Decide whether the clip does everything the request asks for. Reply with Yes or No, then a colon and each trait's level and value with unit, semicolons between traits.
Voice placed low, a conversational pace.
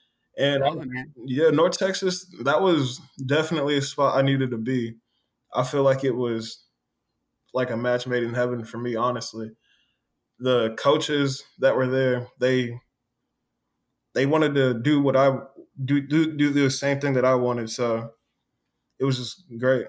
Yes: low, 130 Hz; average, 165 wpm